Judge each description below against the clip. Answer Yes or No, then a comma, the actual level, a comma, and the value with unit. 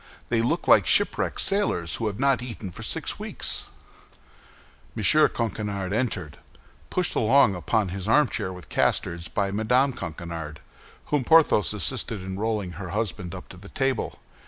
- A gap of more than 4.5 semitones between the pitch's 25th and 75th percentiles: Yes, average, 5.0 semitones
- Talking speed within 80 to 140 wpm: No, average, 150 wpm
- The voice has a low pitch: Yes, low, 105 Hz